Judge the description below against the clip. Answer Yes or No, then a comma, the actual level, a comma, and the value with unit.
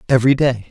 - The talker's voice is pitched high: No, low, 125 Hz